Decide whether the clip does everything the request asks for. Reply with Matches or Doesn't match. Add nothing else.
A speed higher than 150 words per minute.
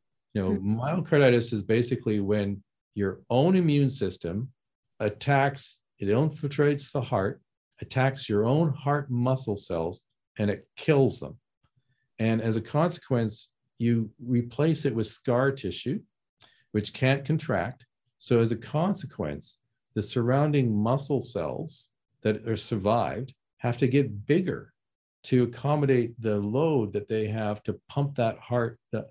Doesn't match